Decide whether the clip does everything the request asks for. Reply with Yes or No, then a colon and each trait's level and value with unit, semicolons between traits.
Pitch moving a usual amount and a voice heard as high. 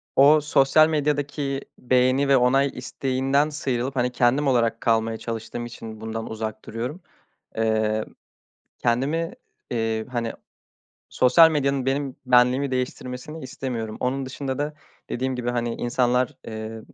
No: average, 3.0 semitones; low, 125 Hz